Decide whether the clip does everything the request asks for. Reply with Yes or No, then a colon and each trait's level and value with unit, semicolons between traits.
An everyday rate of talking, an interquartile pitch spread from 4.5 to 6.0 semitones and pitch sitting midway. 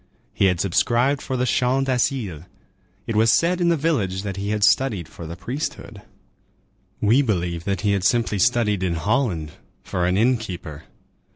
No: average, 175 wpm; wide, 5.6 semitones; low, 105 Hz